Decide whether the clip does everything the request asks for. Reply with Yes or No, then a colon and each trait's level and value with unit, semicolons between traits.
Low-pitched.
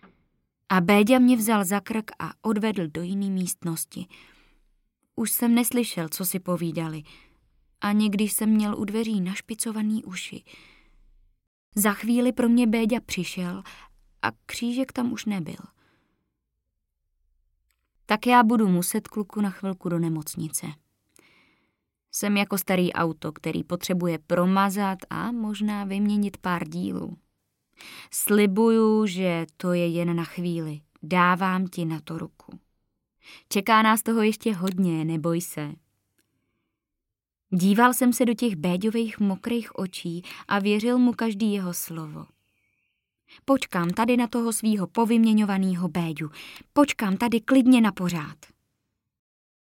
No: high, 195 Hz